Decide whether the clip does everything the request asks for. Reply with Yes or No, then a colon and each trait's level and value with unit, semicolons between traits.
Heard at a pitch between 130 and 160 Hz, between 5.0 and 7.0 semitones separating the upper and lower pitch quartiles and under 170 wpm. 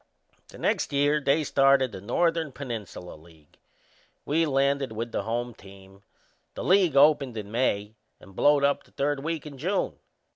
Yes: low, 135 Hz; wide, 5.5 semitones; average, 160 wpm